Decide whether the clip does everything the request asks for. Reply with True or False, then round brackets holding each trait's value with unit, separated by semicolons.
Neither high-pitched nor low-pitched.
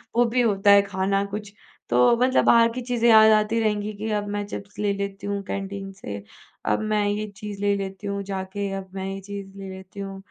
False (200 Hz)